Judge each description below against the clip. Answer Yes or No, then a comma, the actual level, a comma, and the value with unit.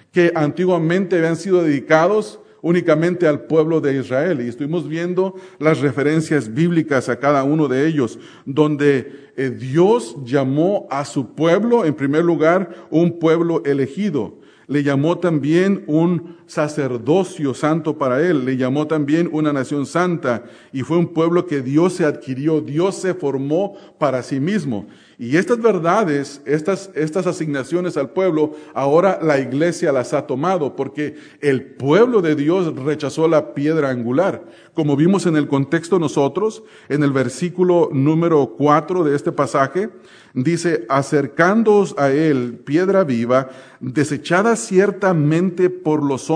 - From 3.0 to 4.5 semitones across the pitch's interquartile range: Yes, average, 3.7 semitones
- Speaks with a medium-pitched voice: Yes, medium, 155 Hz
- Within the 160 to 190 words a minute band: No, average, 140 wpm